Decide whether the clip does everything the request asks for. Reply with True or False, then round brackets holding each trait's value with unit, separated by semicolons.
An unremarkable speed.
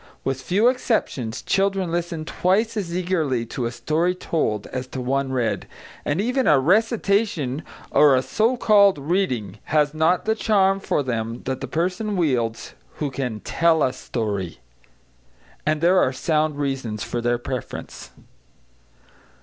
True (150 wpm)